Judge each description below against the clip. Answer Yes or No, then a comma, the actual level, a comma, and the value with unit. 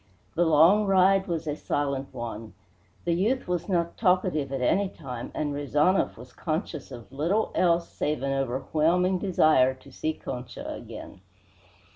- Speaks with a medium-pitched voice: Yes, medium, 155 Hz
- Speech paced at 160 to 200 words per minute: No, average, 150 wpm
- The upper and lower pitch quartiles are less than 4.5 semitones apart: No, average, 5.0 semitones